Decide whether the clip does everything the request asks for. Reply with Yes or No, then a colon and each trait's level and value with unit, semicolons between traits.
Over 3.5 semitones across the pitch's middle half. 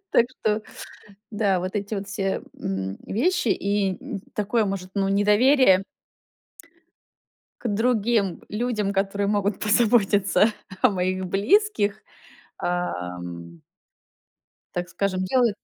No: narrow, 2.5 semitones